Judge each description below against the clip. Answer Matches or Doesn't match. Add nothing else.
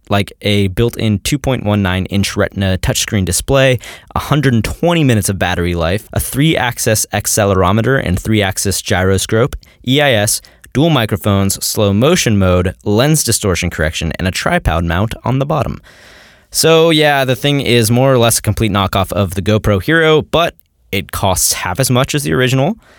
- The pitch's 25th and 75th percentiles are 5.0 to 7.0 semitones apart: Matches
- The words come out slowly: Doesn't match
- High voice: Doesn't match